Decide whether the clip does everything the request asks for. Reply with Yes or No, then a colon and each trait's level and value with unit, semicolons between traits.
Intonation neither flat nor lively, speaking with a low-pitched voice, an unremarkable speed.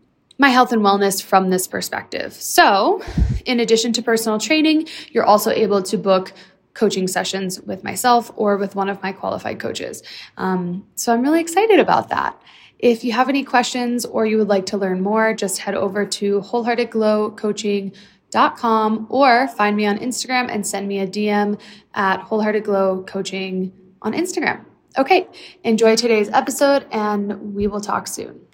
No: average, 3.4 semitones; high, 210 Hz; average, 160 wpm